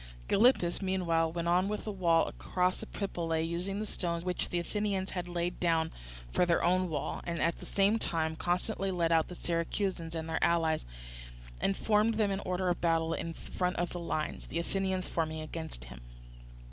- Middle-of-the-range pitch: Yes, medium, 175 Hz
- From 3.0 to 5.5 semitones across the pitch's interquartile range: No, narrow, 2.4 semitones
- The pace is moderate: Yes, average, 185 wpm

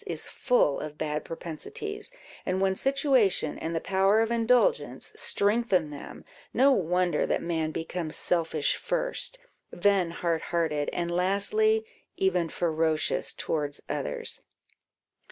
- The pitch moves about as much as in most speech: No, wide, 6.4 semitones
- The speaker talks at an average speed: No, slow, 120 wpm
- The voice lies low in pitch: No, medium, 180 Hz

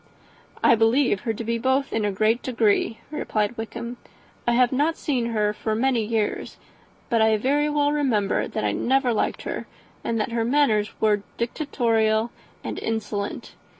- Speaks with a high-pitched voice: Yes, high, 230 Hz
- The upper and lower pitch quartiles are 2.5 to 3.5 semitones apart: Yes, average, 3.1 semitones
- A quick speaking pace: No, average, 165 wpm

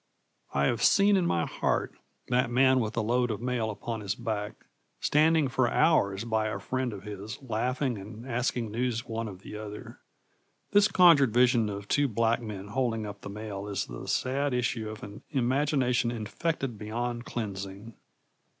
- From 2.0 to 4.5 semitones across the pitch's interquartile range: Yes, average, 3.4 semitones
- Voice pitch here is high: No, low, 115 Hz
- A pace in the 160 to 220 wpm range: Yes, average, 170 wpm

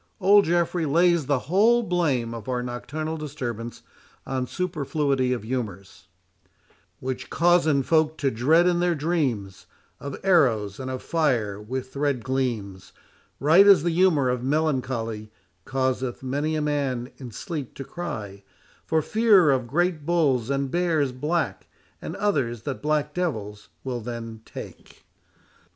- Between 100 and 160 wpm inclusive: Yes, average, 140 wpm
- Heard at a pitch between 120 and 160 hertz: Yes, medium, 140 Hz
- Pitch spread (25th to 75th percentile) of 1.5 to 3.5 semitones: No, average, 5.0 semitones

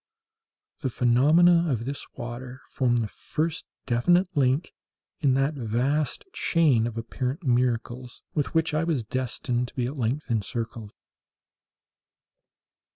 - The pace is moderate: No, slow, 125 wpm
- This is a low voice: Yes, low, 130 Hz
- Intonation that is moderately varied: Yes, average, 4.1 semitones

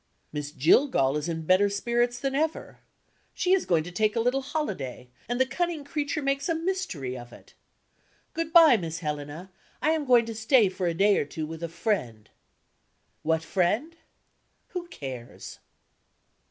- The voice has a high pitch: Yes, high, 210 Hz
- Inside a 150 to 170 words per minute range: Yes, average, 165 wpm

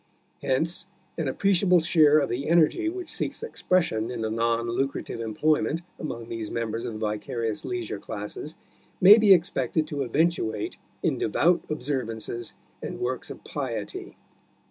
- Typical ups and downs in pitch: No, wide, 6.8 semitones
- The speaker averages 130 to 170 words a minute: Yes, average, 145 wpm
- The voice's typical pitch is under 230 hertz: Yes, medium, 140 Hz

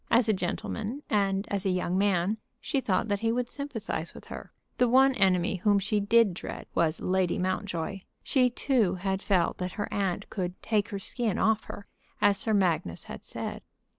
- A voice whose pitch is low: No, high, 200 Hz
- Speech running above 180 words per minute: Yes, average, 190 wpm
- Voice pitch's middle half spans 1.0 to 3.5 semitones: Yes, average, 3.2 semitones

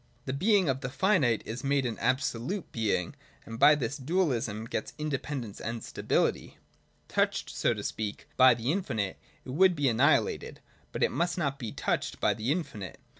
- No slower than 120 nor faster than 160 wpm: No, average, 175 wpm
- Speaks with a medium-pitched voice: No, low, 130 Hz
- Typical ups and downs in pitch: Yes, average, 4.9 semitones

